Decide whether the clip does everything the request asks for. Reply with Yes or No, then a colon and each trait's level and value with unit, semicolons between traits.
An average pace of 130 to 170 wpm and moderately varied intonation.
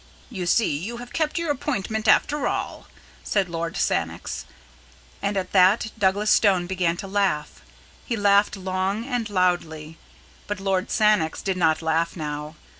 Yes: average, 150 wpm; average, 3.7 semitones